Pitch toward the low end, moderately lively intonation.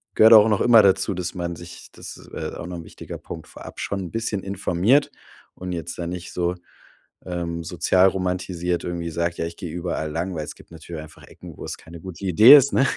No: very low, 90 Hz; narrow, 2.3 semitones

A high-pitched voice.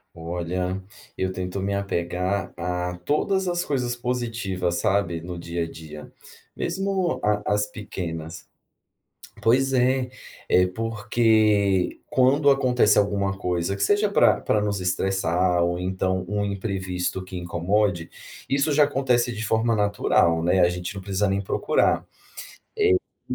No: low, 100 Hz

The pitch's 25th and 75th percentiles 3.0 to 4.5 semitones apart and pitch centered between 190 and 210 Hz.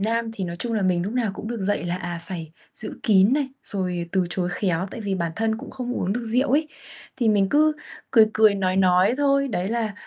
Yes: average, 4.2 semitones; high, 205 Hz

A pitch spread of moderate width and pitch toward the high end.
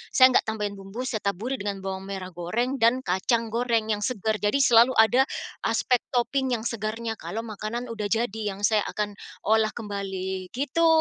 Yes: average, 3.1 semitones; high, 220 Hz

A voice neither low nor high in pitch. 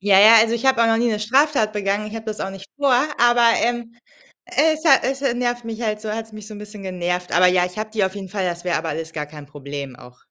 No: high, 210 Hz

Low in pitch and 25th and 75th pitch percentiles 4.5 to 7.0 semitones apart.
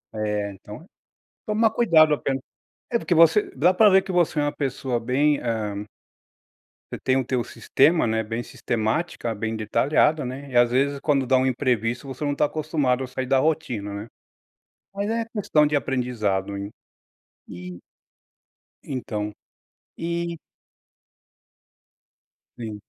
Yes: low, 130 Hz; wide, 5.6 semitones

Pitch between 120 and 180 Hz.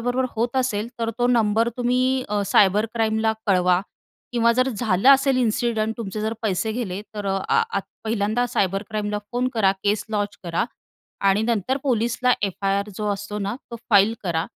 No: high, 220 Hz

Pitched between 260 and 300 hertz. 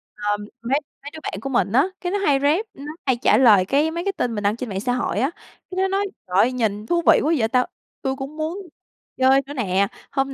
Yes: very high, 265 Hz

